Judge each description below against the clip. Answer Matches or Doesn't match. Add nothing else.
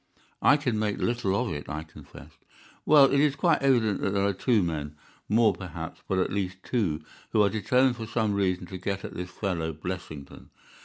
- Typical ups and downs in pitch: Matches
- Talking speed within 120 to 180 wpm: Doesn't match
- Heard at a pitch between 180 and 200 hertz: Doesn't match